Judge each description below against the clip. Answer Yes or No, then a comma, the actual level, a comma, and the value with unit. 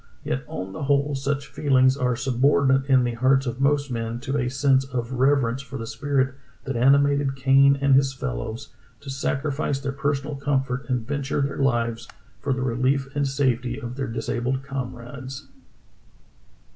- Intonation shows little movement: Yes, narrow, 1.9 semitones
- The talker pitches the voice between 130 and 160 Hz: Yes, low, 135 Hz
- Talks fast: No, average, 165 wpm